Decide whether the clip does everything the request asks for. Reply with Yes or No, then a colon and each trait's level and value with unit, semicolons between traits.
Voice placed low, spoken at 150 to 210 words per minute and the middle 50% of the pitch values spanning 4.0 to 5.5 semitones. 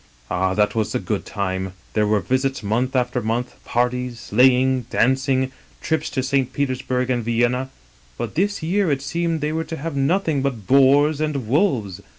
No: low, 130 Hz; average, 180 wpm; average, 3.2 semitones